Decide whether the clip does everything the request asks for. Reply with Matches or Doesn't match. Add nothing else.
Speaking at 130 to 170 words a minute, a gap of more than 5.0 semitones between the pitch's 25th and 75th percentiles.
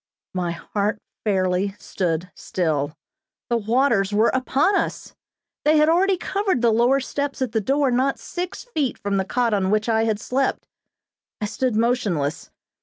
Matches